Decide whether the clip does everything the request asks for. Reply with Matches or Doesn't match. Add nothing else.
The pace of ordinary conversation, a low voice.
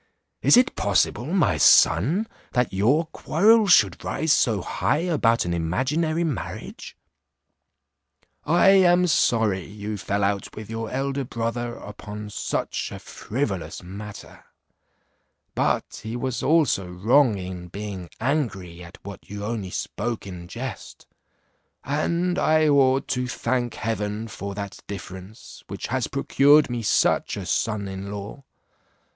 Doesn't match